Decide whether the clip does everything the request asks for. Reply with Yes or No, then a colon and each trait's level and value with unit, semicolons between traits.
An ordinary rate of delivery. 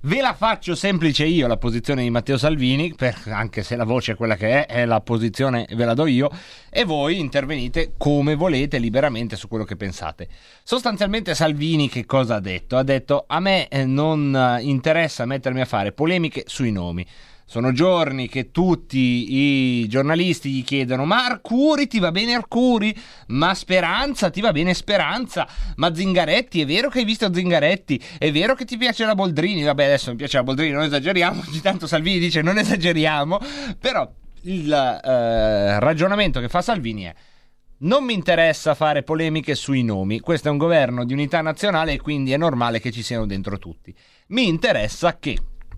No: fast, 180 wpm